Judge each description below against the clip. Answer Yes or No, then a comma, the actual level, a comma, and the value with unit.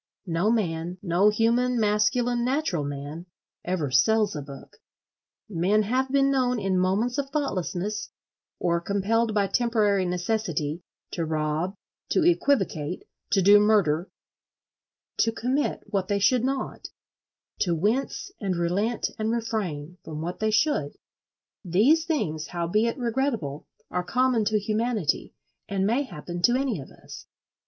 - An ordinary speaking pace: No, slow, 130 wpm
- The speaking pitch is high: Yes, high, 205 Hz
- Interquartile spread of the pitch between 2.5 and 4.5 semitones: No, average, 5.3 semitones